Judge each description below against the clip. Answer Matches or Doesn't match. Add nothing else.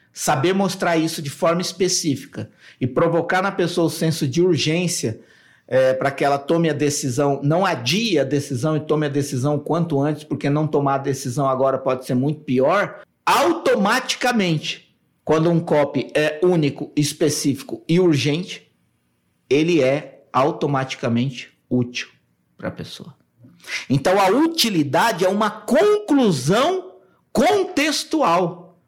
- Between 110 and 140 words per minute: Matches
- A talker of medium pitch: Matches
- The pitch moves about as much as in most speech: Matches